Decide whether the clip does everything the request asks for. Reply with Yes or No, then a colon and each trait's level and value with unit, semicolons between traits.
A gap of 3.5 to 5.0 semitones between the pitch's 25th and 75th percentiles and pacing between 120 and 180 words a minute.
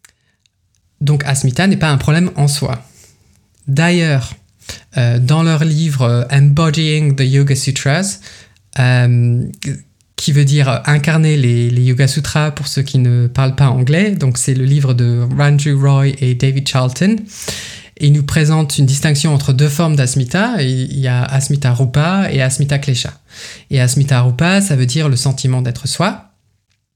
No: average, 2.9 semitones; average, 160 wpm